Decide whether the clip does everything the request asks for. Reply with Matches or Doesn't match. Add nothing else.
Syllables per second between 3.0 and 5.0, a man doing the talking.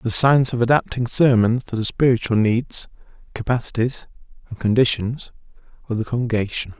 Doesn't match